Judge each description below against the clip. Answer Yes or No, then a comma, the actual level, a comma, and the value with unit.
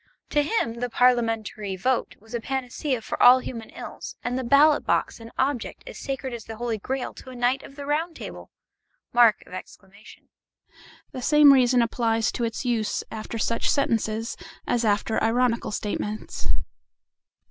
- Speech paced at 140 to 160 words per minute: Yes, average, 155 wpm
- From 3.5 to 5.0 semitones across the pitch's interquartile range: No, average, 2.8 semitones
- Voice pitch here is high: Yes, high, 240 Hz